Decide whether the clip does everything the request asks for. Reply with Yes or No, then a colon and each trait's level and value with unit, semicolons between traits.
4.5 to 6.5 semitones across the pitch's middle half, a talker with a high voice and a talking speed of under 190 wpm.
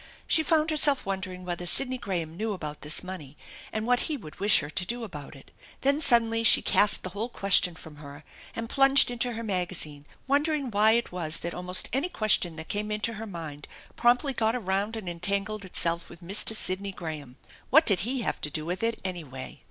No: wide, 5.4 semitones; high, 195 Hz; fast, 205 wpm